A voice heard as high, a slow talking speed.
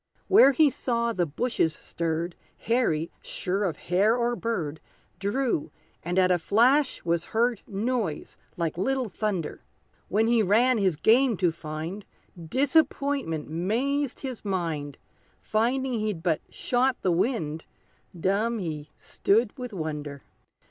Yes: high, 205 Hz; slow, 130 wpm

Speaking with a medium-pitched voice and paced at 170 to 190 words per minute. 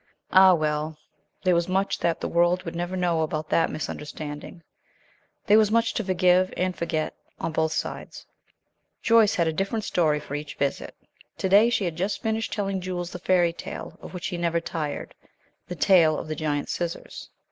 Yes: medium, 175 Hz; average, 185 wpm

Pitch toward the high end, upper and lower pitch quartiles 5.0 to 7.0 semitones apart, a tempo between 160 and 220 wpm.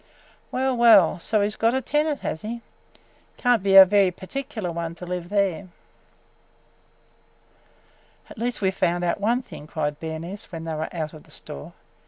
Yes: high, 195 Hz; wide, 5.6 semitones; average, 180 wpm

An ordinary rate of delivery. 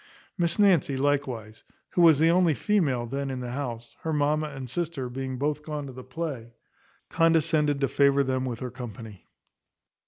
Yes: average, 175 wpm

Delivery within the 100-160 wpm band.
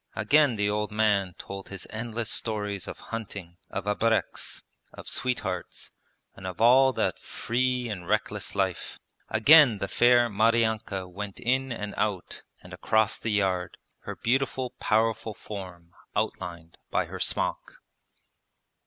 Yes: slow, 135 wpm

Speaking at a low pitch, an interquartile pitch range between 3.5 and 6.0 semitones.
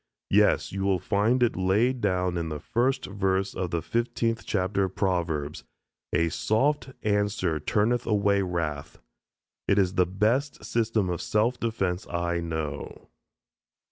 Yes: very low, 95 Hz; average, 4.0 semitones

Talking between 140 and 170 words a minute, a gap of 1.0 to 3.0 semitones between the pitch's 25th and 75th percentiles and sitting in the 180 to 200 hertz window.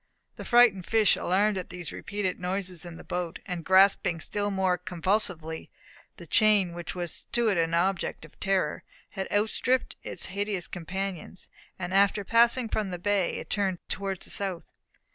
Yes: average, 165 wpm; narrow, 2.4 semitones; high, 190 Hz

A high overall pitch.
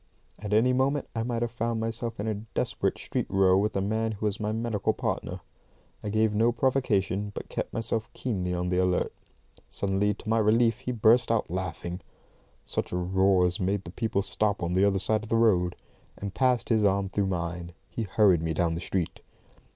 No: low, 105 Hz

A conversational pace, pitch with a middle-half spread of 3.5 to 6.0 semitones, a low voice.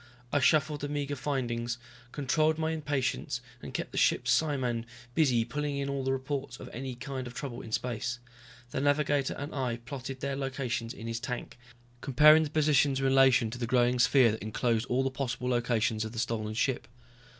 No: average, 190 wpm; average, 2.9 semitones; low, 130 Hz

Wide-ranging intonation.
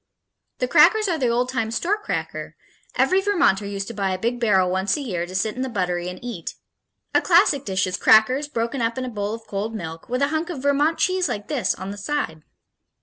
Yes: wide, 6.6 semitones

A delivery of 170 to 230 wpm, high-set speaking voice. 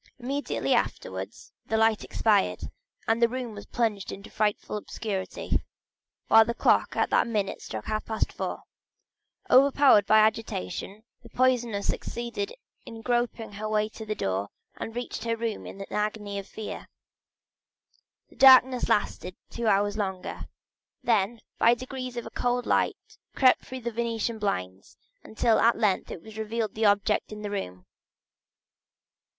No: average, 145 wpm; high, 220 Hz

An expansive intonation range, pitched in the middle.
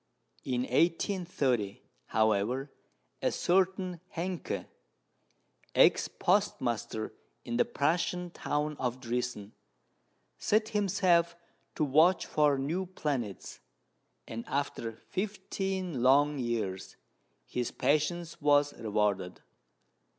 Yes: wide, 6.9 semitones; medium, 145 Hz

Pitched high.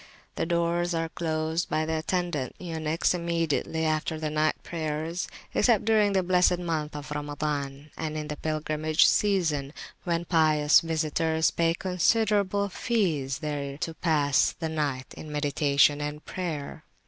No: medium, 160 Hz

